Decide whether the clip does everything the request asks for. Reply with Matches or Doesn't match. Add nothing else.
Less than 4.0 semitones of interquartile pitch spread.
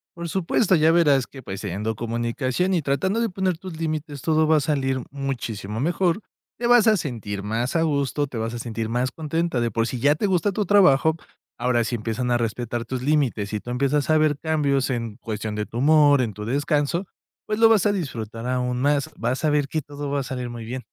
Doesn't match